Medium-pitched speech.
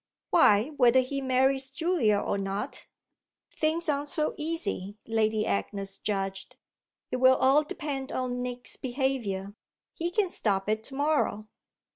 No: very high, 255 Hz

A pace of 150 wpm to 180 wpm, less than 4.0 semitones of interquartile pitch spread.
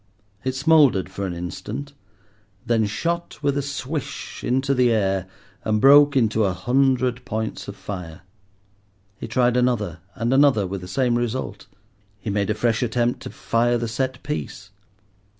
No: average, 155 wpm; average, 4.4 semitones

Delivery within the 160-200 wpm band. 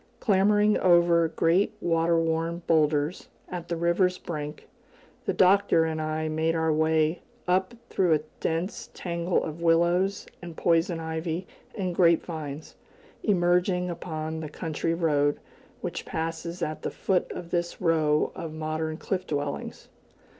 No: average, 140 wpm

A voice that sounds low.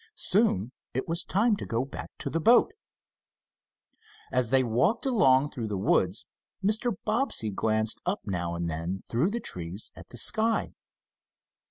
Yes: low, 130 Hz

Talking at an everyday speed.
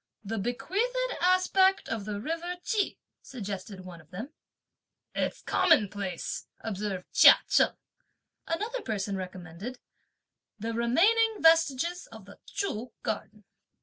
No: slow, 115 wpm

